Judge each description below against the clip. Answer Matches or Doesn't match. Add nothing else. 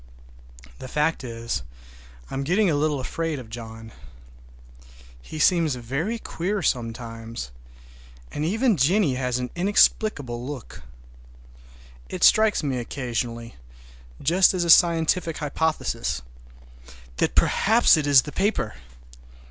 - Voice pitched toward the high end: Doesn't match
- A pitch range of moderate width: Doesn't match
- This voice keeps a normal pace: Doesn't match